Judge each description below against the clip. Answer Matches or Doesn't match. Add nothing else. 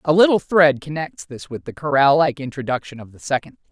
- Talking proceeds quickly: Matches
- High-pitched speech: Doesn't match